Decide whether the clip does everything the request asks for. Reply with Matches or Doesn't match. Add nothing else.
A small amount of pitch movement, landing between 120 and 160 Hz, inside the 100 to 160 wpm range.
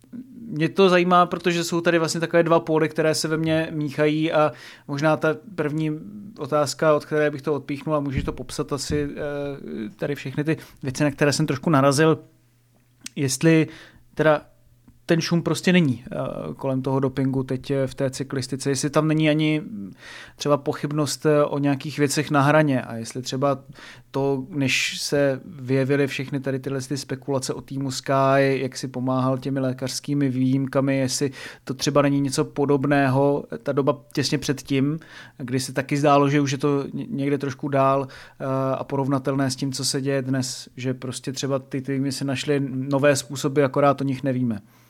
Doesn't match